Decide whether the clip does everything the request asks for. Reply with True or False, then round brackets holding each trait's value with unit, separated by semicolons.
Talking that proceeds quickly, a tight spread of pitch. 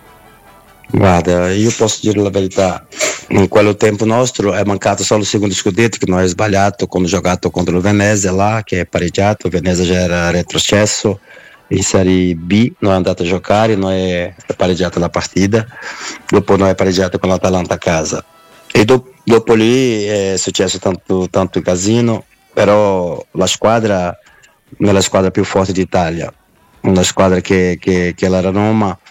True (175 wpm; 2.3 semitones)